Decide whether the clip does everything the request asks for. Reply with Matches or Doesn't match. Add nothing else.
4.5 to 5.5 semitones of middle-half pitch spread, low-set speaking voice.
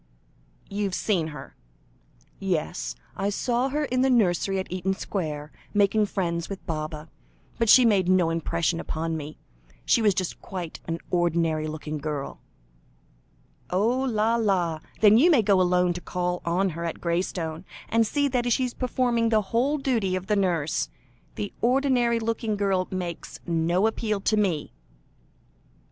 Doesn't match